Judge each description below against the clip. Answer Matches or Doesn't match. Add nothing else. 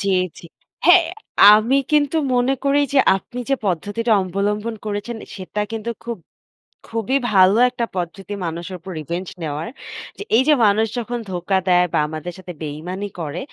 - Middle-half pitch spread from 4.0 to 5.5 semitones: Matches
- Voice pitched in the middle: Doesn't match